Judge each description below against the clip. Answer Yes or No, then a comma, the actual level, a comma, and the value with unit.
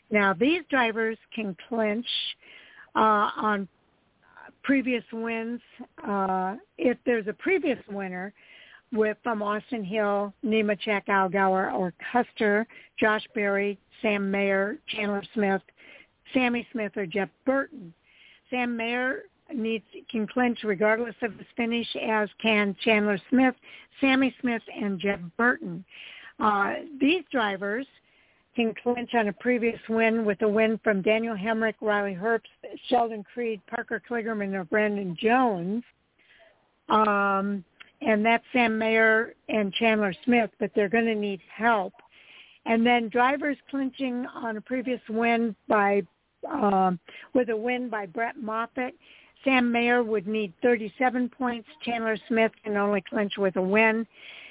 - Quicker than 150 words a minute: No, slow, 135 wpm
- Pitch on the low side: No, high, 225 Hz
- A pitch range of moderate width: Yes, average, 3.0 semitones